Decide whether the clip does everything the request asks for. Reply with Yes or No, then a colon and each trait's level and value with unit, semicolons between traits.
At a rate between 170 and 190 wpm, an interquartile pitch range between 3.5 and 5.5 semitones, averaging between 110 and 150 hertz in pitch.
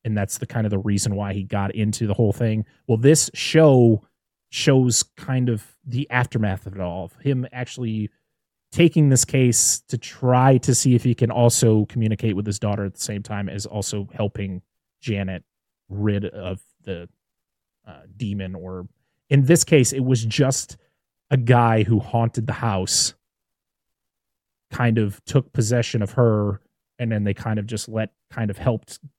Yes: average, 175 wpm; average, 3.8 semitones; low, 115 Hz